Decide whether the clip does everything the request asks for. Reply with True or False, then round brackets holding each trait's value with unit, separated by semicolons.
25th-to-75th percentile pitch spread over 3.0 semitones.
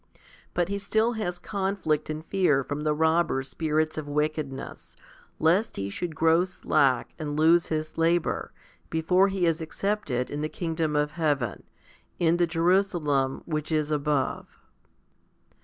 False (2.7 semitones)